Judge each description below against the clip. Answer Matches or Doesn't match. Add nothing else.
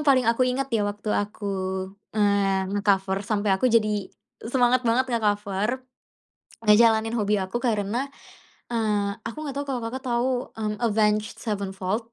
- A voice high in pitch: Matches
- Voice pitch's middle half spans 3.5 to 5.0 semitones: Doesn't match